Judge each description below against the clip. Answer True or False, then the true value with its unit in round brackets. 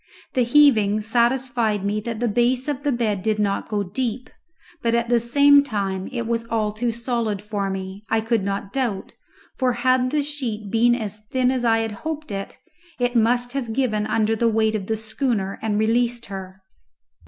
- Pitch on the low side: False (230 Hz)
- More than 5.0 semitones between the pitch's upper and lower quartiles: False (2.7 semitones)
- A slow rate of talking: False (190 wpm)